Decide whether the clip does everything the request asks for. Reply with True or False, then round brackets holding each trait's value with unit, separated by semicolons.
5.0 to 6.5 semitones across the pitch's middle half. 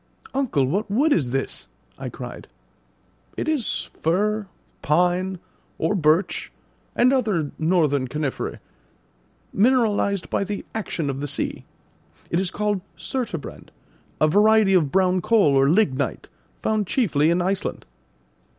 True (5.6 semitones)